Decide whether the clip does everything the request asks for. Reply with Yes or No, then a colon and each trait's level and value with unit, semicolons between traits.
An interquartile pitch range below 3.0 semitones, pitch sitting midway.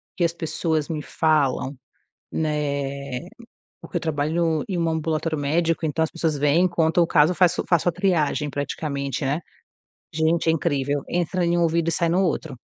Yes: narrow, 2.5 semitones; medium, 160 Hz